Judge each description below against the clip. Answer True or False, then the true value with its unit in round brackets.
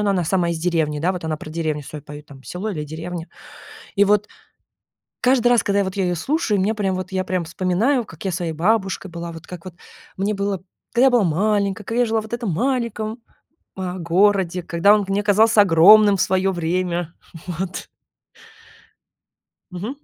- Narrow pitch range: False (3.6 semitones)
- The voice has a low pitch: False (190 Hz)